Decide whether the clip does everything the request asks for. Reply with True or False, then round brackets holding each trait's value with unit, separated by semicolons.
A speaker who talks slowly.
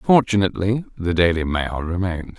True (125 wpm)